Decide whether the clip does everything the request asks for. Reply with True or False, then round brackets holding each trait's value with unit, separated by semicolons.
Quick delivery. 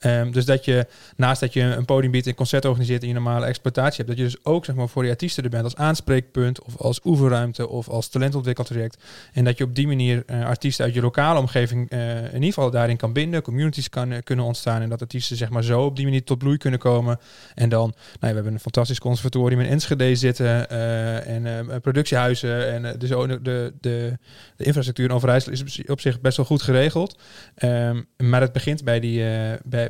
True (235 wpm)